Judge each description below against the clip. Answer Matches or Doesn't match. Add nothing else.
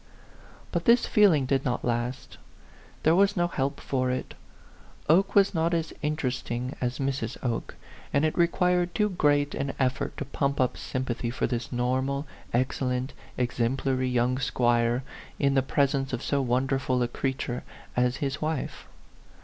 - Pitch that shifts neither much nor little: Matches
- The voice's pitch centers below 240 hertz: Matches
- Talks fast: Doesn't match